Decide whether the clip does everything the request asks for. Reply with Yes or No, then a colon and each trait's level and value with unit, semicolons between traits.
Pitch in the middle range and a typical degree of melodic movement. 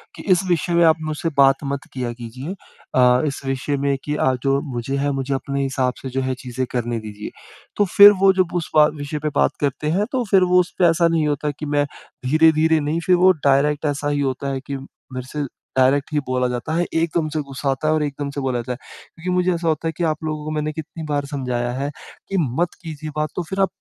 Yes: medium, 145 Hz; average, 3.4 semitones